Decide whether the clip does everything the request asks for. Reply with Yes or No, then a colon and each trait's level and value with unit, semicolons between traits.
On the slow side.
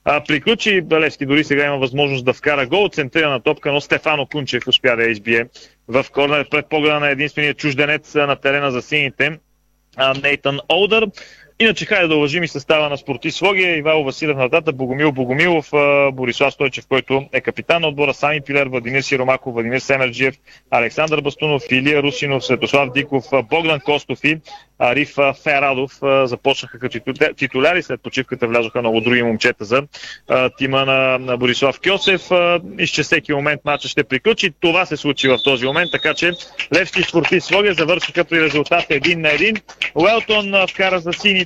No: average, 160 wpm